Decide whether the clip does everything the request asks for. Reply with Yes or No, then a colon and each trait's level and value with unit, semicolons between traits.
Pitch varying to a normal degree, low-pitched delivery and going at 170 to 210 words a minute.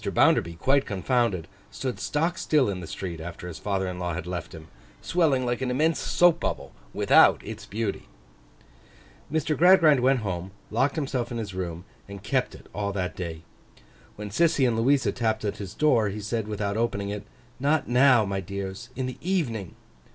No: wide, 5.8 semitones; low, 110 Hz; average, 180 wpm